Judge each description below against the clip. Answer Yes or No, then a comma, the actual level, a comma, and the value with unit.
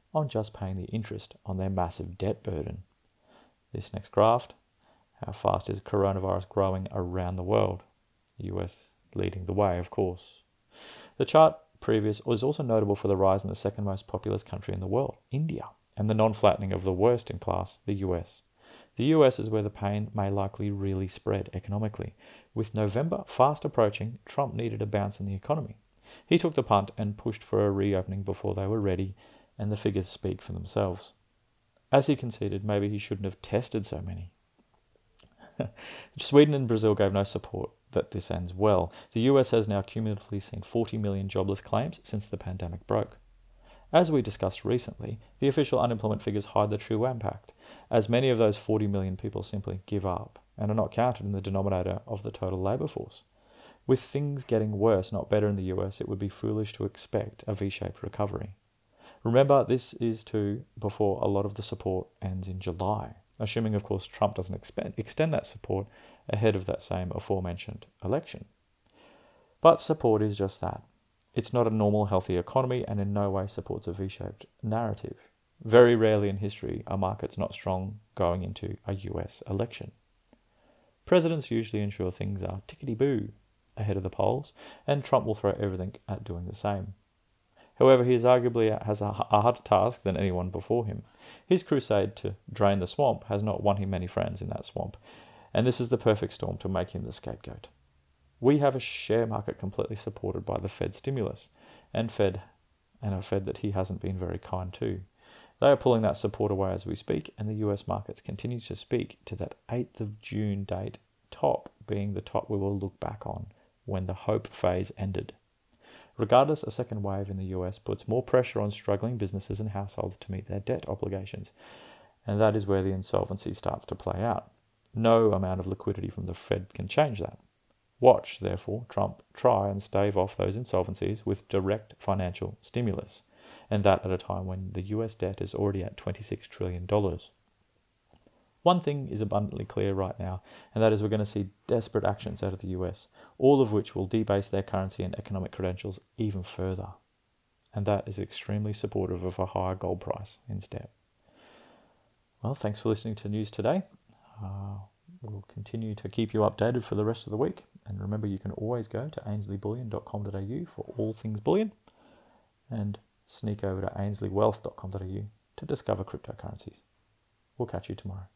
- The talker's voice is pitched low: Yes, low, 105 Hz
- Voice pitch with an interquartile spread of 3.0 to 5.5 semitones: No, narrow, 2.6 semitones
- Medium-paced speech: Yes, average, 185 wpm